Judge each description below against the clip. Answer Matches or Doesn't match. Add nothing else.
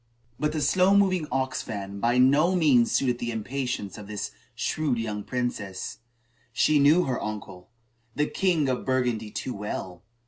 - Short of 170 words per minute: Matches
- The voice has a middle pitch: Doesn't match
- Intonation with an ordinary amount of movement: Doesn't match